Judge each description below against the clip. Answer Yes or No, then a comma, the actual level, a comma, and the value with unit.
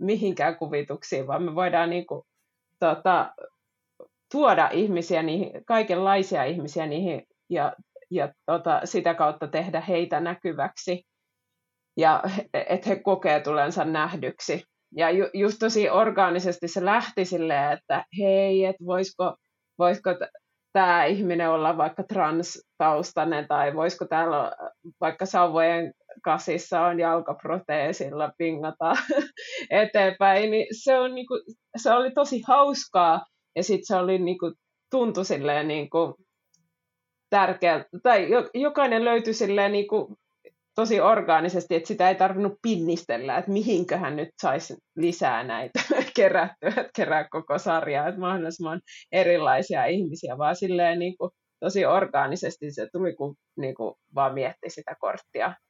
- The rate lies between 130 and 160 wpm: No, average, 120 wpm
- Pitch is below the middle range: No, medium, 180 Hz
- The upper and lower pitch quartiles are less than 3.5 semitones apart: No, average, 3.8 semitones